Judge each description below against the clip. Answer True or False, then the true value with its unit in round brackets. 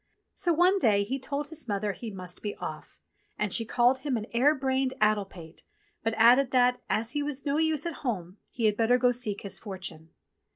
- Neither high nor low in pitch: False (240 Hz)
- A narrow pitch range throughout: False (4.9 semitones)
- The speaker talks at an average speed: False (210 wpm)